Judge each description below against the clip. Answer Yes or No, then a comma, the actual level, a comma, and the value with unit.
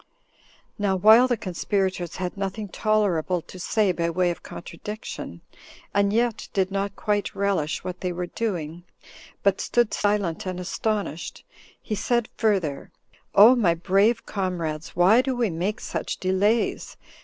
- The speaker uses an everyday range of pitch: Yes, average, 3.3 semitones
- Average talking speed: Yes, average, 145 wpm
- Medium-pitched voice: No, high, 195 Hz